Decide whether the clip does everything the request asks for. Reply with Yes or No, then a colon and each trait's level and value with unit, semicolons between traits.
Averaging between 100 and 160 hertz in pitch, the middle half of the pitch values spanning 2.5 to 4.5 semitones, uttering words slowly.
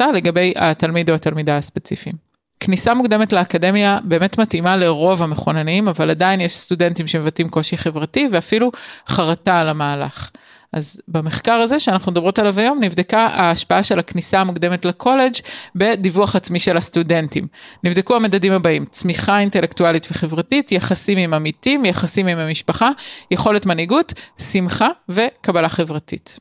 No: medium, 180 Hz; average, 3.3 semitones; slow, 130 wpm